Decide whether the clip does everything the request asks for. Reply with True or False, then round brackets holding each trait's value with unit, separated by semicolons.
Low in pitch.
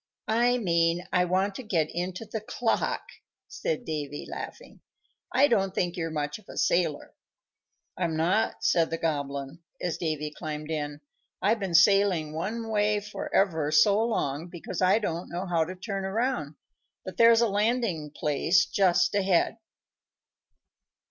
False (180 Hz)